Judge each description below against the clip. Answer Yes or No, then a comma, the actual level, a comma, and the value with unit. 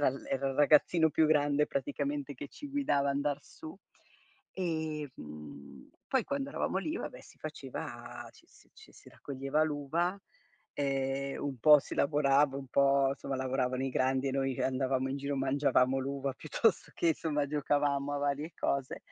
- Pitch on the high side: No, medium, 140 Hz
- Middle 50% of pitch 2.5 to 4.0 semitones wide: No, narrow, 1.9 semitones